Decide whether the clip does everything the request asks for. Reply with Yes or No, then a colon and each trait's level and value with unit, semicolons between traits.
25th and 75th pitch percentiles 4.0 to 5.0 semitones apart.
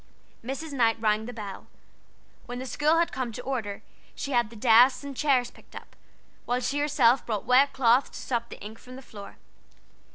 No: average, 3.1 semitones